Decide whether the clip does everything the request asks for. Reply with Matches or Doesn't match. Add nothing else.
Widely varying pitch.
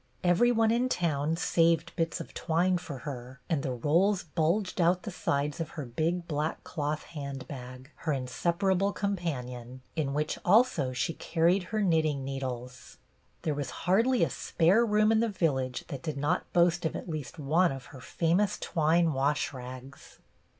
Doesn't match